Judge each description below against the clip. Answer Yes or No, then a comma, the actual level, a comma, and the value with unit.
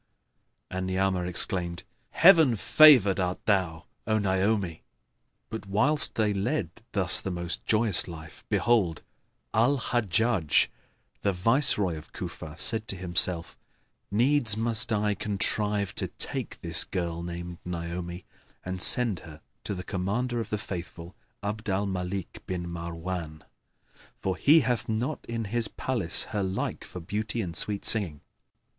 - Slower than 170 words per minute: Yes, average, 140 wpm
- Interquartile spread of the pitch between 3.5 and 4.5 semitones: Yes, average, 4.0 semitones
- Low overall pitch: Yes, very low, 95 Hz